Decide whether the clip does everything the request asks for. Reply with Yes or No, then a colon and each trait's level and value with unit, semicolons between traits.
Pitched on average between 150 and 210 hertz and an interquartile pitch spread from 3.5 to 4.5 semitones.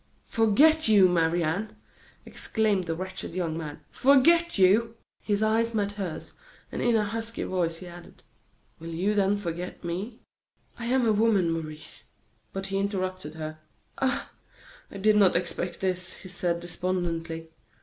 Yes: high, 190 Hz; average, 4.1 semitones